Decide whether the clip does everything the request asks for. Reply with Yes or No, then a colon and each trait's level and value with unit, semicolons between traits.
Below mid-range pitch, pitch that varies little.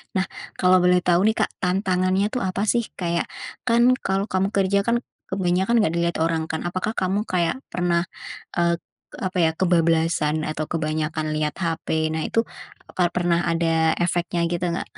No: medium, 175 Hz; narrow, 2.1 semitones